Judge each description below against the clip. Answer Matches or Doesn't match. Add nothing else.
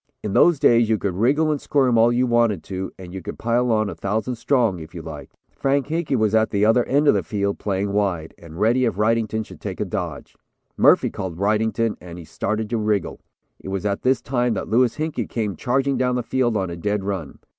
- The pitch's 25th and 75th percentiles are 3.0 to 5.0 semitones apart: Matches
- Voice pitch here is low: Matches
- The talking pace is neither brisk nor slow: Doesn't match